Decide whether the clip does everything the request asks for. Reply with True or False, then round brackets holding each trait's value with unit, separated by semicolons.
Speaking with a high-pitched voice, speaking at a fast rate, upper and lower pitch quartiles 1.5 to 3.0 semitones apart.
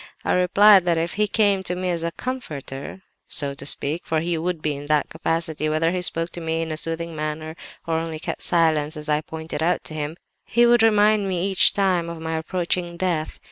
False (165 Hz; 225 wpm; 2.6 semitones)